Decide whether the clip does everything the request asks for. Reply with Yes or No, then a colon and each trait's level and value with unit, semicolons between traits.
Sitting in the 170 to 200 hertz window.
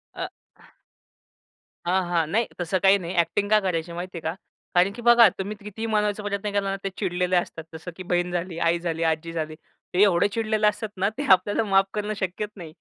Yes: high, 190 Hz